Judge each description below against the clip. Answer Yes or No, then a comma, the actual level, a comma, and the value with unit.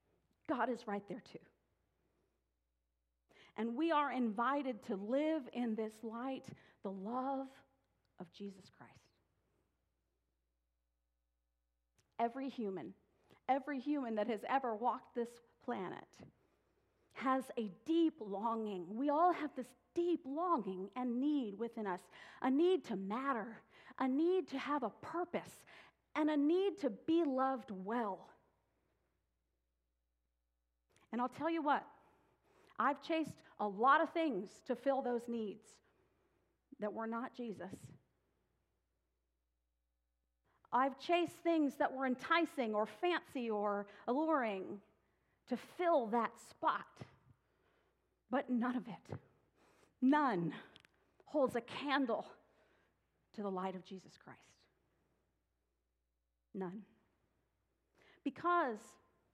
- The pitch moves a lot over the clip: Yes, wide, 6.8 semitones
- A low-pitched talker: No, high, 235 Hz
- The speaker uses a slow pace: Yes, slow, 110 wpm